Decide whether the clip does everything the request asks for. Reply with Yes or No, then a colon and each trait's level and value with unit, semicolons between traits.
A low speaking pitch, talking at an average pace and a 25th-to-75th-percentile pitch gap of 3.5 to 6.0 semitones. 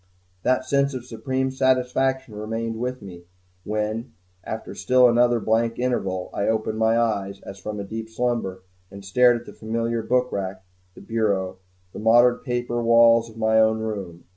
No: low, 115 Hz; average, 165 wpm; narrow, 2.5 semitones